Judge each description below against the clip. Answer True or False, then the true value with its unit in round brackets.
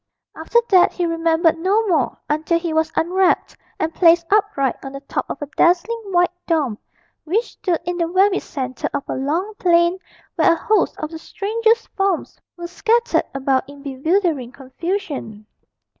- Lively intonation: False (4.5 semitones)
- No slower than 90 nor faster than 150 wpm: False (165 wpm)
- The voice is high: True (335 Hz)